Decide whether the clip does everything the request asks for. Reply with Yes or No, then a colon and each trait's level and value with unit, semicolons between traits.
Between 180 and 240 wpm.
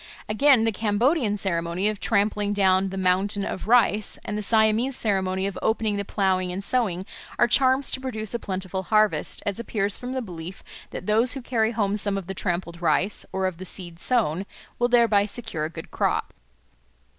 Yes: average, 190 wpm